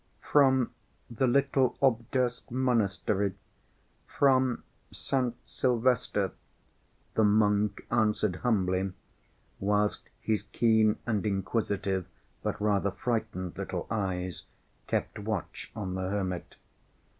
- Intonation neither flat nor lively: Yes, average, 3.8 semitones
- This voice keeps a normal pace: No, slow, 95 wpm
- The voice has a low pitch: Yes, low, 105 Hz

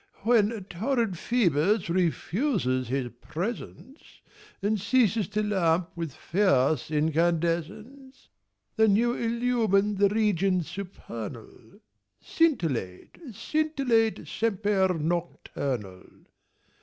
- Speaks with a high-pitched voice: Yes, high, 195 Hz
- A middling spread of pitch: No, wide, 5.7 semitones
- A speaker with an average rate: No, slow, 80 wpm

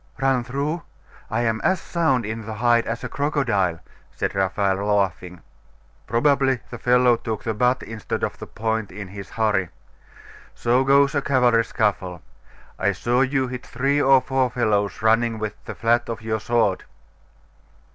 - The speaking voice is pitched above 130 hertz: No, low, 115 Hz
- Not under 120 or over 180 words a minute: Yes, average, 160 wpm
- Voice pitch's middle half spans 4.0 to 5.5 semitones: No, average, 3.6 semitones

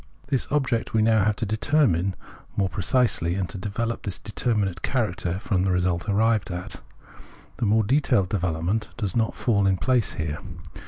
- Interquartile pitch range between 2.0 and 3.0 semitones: No, average, 3.8 semitones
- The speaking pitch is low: Yes, low, 100 Hz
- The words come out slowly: No, average, 170 wpm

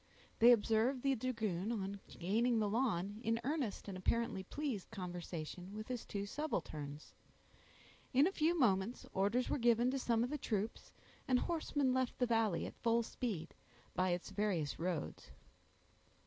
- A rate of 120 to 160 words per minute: Yes, average, 155 wpm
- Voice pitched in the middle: No, high, 225 Hz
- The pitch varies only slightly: No, average, 4.7 semitones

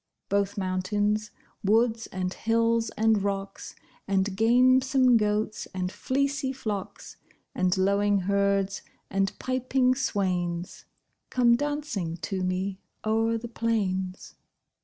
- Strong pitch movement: No, average, 3.4 semitones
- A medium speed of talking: No, slow, 105 wpm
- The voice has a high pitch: Yes, high, 205 Hz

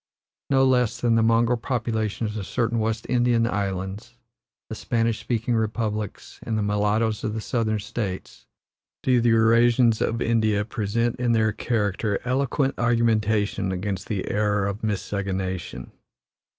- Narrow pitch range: Yes, narrow, 2.3 semitones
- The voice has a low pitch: Yes, low, 110 Hz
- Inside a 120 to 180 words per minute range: Yes, average, 140 wpm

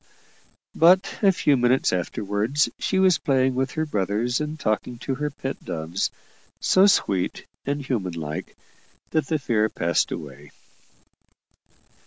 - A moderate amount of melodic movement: No, wide, 6.5 semitones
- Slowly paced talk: Yes, slow, 130 wpm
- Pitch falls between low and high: No, low, 130 Hz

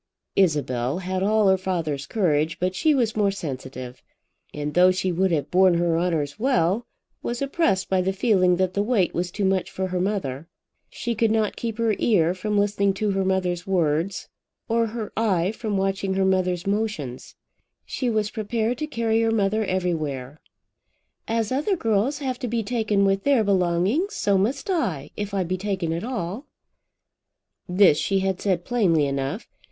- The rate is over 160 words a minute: Yes, average, 175 wpm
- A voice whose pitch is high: Yes, high, 195 Hz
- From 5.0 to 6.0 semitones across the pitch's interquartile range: No, average, 3.8 semitones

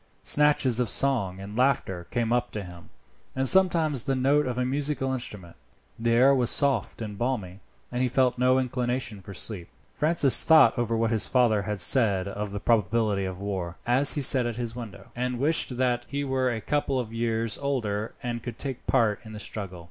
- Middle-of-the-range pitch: No, low, 120 Hz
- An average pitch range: Yes, average, 3.9 semitones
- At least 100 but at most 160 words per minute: No, average, 200 wpm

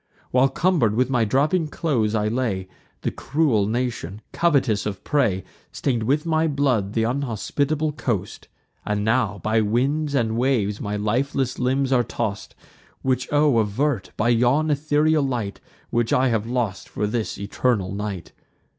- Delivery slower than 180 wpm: Yes, average, 150 wpm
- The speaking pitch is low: Yes, low, 120 Hz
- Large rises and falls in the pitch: No, average, 4.6 semitones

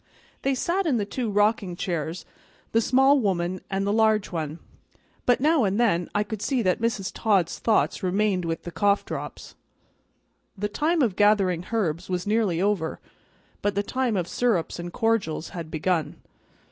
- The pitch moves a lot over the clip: No, average, 4.3 semitones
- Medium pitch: No, high, 205 Hz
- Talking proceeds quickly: No, average, 170 wpm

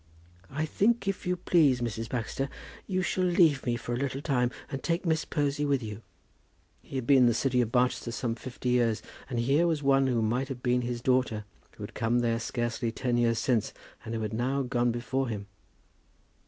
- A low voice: Yes, low, 125 Hz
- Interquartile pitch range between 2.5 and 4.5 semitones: Yes, average, 2.9 semitones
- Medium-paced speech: No, fast, 210 wpm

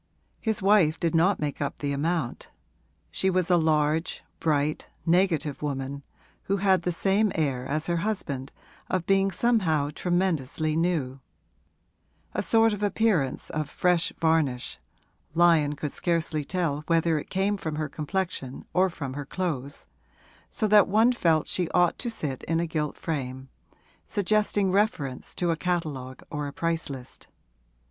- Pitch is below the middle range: No, medium, 165 Hz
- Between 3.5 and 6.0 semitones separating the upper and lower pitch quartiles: Yes, average, 4.3 semitones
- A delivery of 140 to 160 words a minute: Yes, average, 150 wpm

